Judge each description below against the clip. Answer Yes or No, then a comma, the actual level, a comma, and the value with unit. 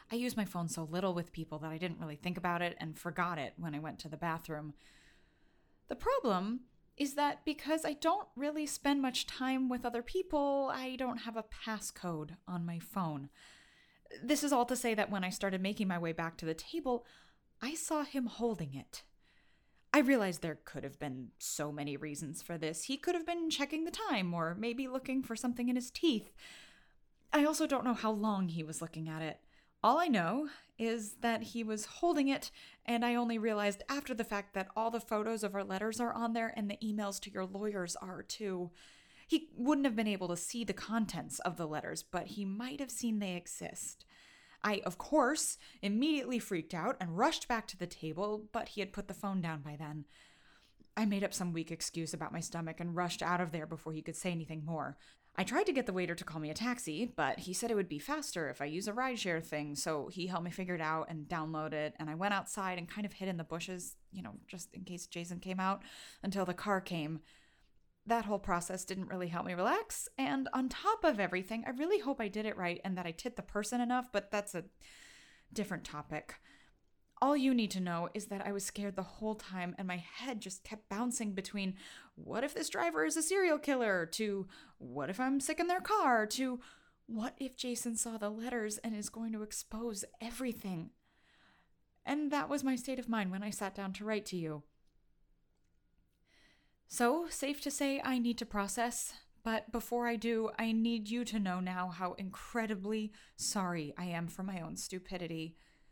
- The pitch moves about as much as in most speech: No, wide, 5.7 semitones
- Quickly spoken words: Yes, fast, 215 wpm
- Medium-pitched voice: No, high, 205 Hz